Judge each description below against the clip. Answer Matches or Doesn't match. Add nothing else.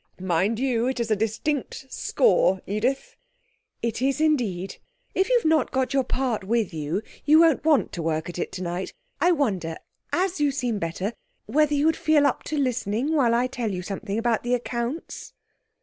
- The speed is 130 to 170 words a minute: Doesn't match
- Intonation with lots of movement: Matches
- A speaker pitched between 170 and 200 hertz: Doesn't match